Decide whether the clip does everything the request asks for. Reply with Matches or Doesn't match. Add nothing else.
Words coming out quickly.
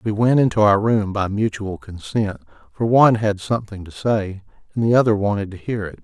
Matches